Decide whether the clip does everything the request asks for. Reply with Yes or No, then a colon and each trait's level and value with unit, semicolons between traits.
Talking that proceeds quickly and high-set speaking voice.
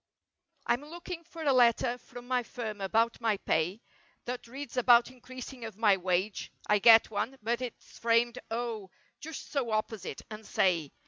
No: average, 150 wpm; high, 235 Hz